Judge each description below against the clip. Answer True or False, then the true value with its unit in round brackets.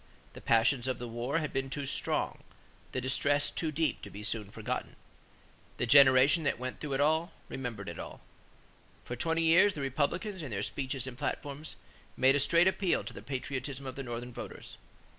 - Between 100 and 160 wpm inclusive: False (190 wpm)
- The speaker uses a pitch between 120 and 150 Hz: True (135 Hz)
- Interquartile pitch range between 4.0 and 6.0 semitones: False (3.6 semitones)